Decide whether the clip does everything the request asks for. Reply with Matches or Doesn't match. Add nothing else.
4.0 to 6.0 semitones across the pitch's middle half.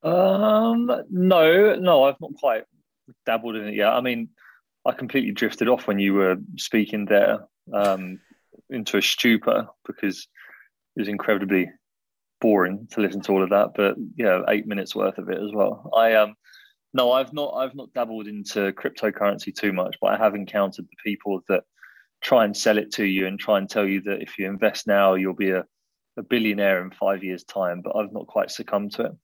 Doesn't match